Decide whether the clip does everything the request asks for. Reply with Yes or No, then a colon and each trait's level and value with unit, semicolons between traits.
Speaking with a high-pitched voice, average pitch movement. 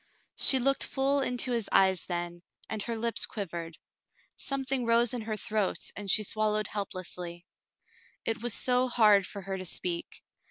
Yes: high, 215 Hz; average, 4.3 semitones